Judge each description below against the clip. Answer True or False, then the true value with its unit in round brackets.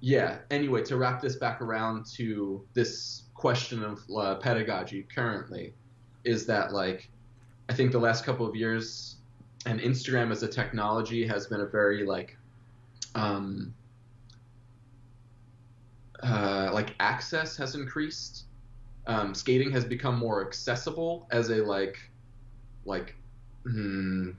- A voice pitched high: False (120 Hz)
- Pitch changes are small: True (1.7 semitones)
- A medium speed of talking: False (125 wpm)